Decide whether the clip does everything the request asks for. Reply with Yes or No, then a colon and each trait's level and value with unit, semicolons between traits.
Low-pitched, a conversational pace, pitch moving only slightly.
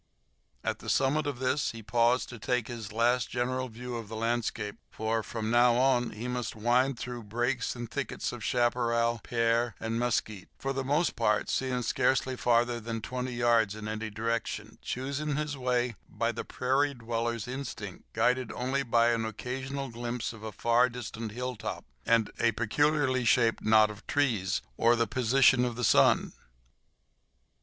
Yes: low, 120 Hz; average, 165 wpm; narrow, 2.0 semitones